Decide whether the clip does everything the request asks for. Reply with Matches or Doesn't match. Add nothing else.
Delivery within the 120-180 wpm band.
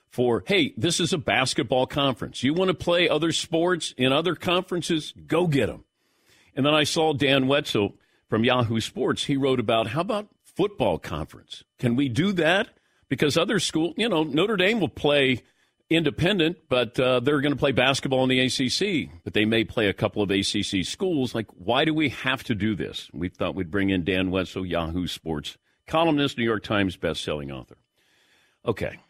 Doesn't match